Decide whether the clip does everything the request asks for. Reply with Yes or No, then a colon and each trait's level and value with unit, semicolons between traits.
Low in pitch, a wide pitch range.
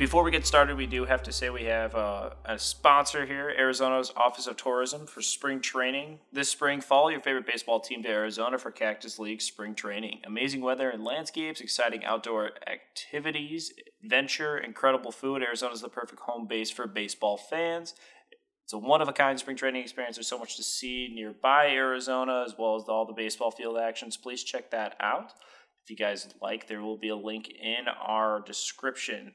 No: low, 125 Hz; average, 4.0 semitones